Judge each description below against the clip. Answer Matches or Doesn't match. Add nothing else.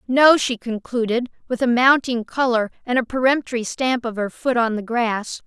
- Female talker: Matches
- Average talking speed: Matches